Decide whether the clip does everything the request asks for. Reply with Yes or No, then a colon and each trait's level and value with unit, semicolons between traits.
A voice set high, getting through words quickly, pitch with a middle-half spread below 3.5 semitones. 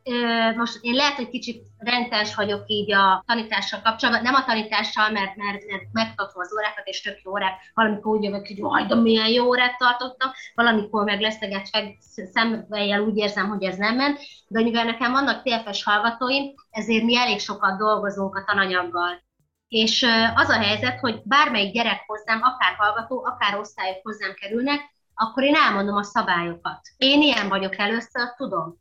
Yes: high, 220 Hz; fast, 165 wpm; average, 2.9 semitones